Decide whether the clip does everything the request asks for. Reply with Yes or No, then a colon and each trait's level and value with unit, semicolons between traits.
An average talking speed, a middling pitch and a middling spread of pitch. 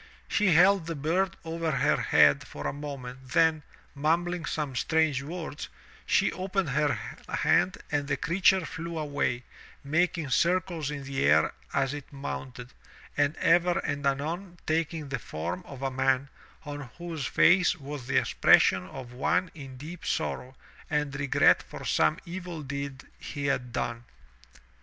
Yes: average, 150 wpm; medium, 145 Hz; average, 3.9 semitones